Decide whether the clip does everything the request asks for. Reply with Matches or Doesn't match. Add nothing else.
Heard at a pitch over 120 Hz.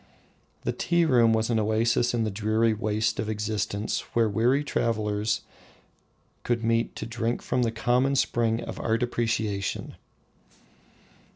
Doesn't match